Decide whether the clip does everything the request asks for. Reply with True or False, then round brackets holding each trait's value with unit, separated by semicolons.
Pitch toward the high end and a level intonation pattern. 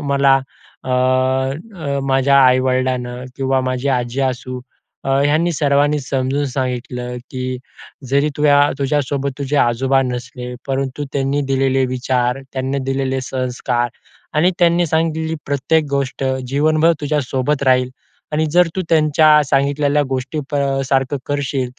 False (135 Hz; 2.1 semitones)